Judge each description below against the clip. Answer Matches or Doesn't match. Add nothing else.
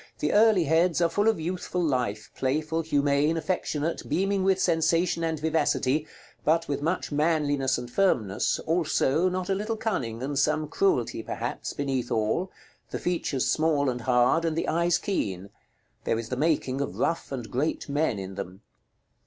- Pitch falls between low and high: Matches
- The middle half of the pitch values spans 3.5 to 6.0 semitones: Matches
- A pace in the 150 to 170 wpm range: Matches